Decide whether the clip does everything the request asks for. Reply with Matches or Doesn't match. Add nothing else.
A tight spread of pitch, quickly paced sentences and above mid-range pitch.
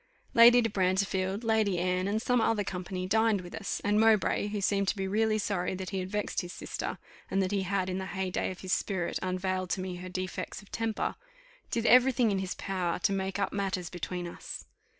Matches